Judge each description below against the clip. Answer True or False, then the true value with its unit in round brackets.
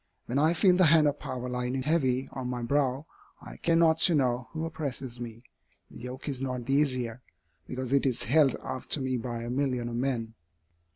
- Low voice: True (130 Hz)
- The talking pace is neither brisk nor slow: False (210 wpm)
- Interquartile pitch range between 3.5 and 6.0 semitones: False (3.0 semitones)